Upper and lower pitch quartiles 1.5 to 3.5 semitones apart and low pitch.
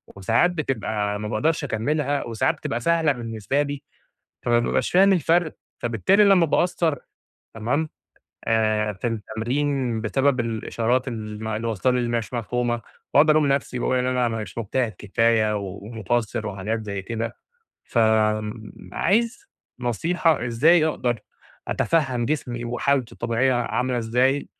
No: average, 4.4 semitones; low, 120 Hz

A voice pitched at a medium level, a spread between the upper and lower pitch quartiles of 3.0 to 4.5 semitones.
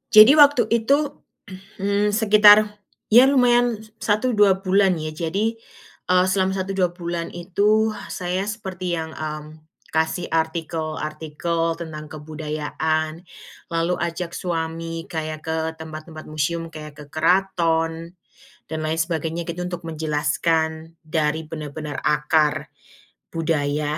Yes: medium, 165 Hz; average, 3.5 semitones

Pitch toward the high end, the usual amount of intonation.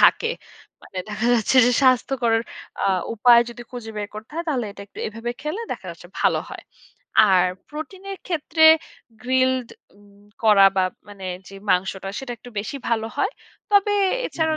No: high, 240 Hz; wide, 6.5 semitones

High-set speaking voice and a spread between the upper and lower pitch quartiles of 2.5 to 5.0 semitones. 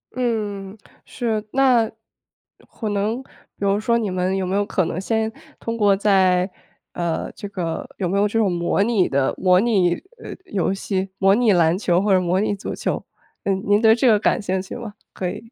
Yes: high, 200 Hz; average, 3.0 semitones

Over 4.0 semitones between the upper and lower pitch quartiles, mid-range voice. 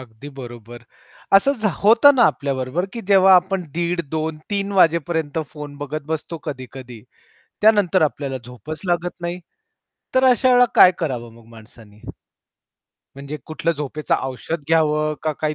Yes: average, 5.1 semitones; medium, 155 Hz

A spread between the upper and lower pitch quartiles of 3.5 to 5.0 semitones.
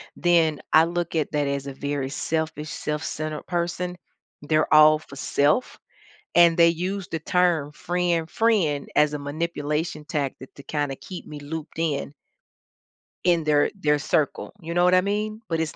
No: average, 2.8 semitones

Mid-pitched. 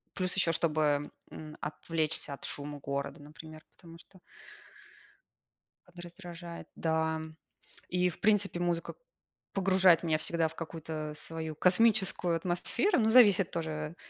Yes: medium, 165 Hz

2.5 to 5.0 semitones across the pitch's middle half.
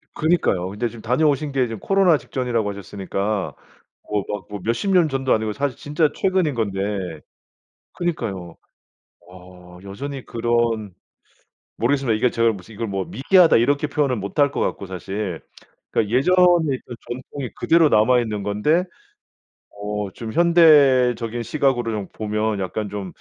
No: wide, 5.6 semitones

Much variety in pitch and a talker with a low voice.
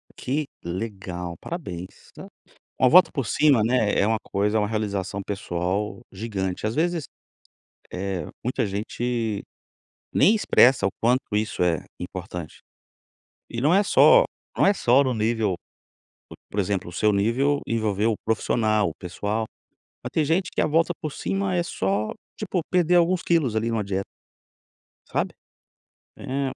Yes: wide, 6.1 semitones; low, 110 Hz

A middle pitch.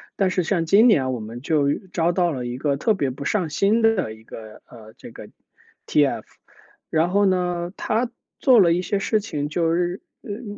Yes: medium, 175 Hz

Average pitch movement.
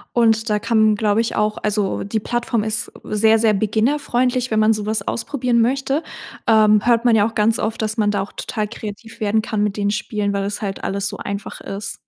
No: narrow, 1.7 semitones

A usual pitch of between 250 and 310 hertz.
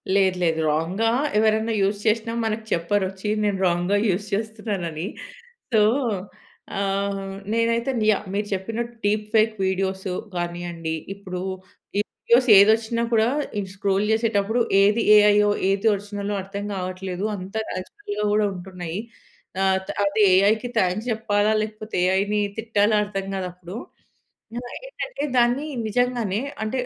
No: high, 205 Hz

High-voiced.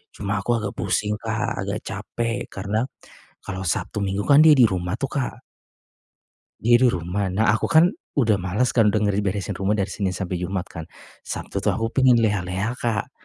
No: low, 105 Hz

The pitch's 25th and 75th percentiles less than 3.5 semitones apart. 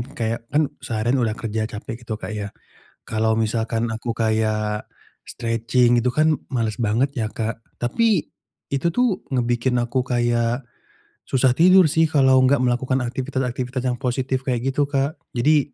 Yes: average, 2.8 semitones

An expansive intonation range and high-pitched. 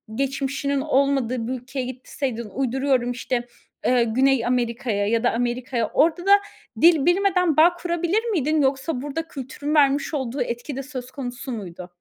No: average, 3.4 semitones; very high, 265 Hz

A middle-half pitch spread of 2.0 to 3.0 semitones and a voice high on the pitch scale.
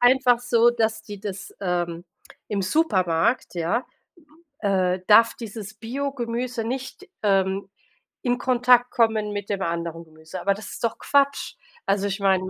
No: average, 4.2 semitones; high, 210 Hz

